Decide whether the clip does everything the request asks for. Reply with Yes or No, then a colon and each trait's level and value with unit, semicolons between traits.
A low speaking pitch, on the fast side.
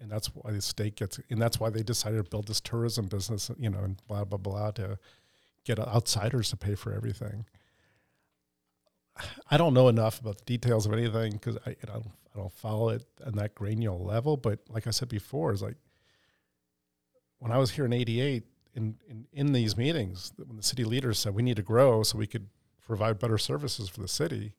Yes: low, 110 Hz; fast, 210 wpm